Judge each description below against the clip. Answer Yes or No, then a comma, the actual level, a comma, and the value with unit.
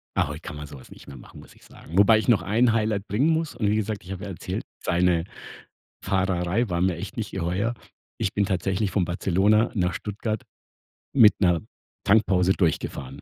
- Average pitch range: Yes, average, 3.6 semitones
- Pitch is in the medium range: No, very low, 95 Hz